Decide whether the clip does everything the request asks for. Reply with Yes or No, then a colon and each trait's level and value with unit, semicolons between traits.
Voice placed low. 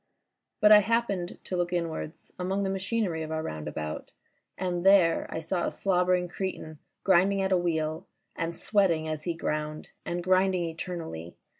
No: medium, 175 Hz